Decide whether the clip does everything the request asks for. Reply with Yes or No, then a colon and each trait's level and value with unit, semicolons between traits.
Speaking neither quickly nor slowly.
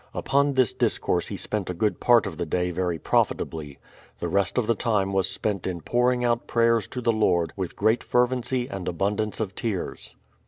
Yes: average, 195 wpm